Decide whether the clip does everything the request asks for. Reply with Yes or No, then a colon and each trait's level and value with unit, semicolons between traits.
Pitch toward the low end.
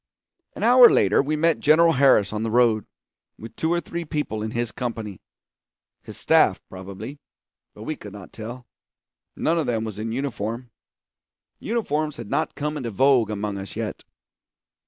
Yes: low, 120 Hz